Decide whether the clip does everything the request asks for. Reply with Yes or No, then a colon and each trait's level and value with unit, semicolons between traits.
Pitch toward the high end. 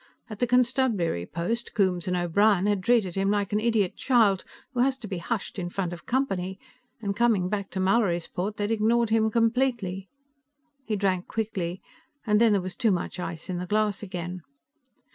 Yes: high, 200 Hz